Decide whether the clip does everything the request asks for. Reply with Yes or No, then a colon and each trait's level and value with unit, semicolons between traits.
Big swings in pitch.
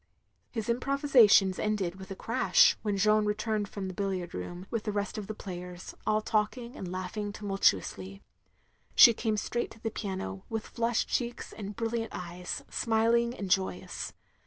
No: average, 3.2 semitones